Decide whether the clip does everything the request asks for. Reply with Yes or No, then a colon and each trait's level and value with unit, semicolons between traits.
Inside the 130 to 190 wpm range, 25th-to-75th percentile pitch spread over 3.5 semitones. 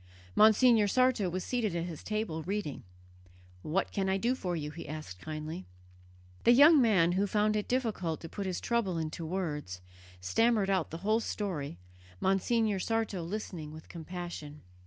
Yes: average, 160 wpm; average, 5.1 semitones